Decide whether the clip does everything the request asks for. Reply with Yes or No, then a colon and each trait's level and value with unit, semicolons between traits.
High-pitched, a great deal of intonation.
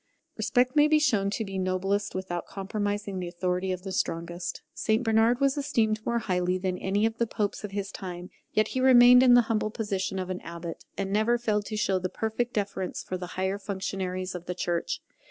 No: high, 200 Hz; average, 3.2 semitones